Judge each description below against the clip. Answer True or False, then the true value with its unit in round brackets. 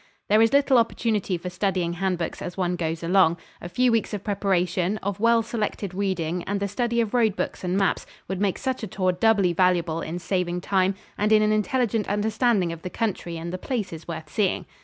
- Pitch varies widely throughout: False (3.5 semitones)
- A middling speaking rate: False (210 wpm)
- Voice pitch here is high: True (195 Hz)